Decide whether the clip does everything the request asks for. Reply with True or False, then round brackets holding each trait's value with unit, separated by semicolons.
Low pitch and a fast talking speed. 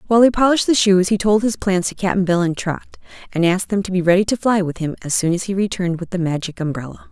False (190 Hz; 280 wpm)